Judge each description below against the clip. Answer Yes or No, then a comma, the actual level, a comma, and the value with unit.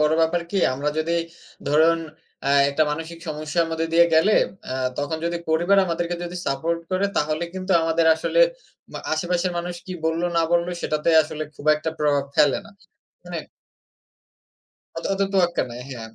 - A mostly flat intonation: Yes, narrow, 2.3 semitones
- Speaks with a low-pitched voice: No, medium, 165 Hz